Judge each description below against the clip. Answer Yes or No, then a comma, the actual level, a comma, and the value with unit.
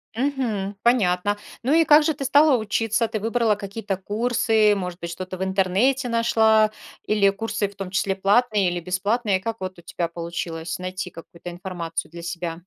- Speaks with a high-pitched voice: Yes, high, 200 Hz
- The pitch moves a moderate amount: Yes, average, 3.9 semitones